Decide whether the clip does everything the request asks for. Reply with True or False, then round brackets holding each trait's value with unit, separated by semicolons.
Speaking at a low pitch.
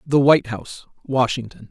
True (125 Hz)